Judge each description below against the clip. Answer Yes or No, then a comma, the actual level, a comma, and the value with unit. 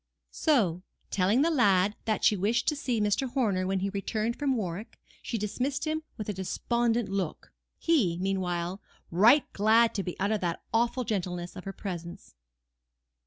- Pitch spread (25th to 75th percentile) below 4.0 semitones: No, average, 4.4 semitones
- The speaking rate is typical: Yes, average, 165 wpm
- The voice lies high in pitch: Yes, high, 210 Hz